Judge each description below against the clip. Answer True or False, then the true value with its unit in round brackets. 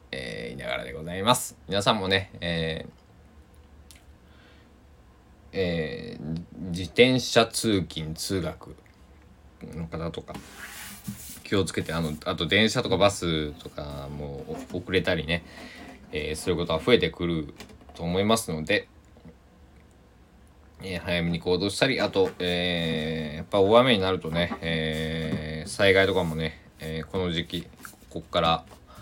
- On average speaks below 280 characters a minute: True (245 characters per minute)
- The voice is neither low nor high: False (80 Hz)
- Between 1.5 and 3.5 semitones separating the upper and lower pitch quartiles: True (2.8 semitones)